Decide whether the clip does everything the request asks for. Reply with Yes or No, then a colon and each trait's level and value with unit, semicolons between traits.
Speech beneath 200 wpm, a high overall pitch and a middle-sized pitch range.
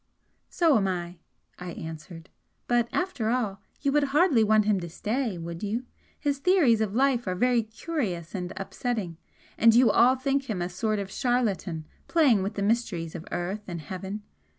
No: average, 175 wpm; high, 215 Hz; wide, 5.7 semitones